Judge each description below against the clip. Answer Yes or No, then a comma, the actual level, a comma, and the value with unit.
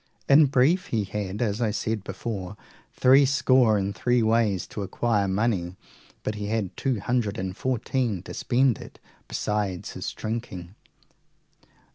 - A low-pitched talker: Yes, low, 110 Hz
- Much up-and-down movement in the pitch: No, average, 3.8 semitones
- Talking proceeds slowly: No, average, 145 wpm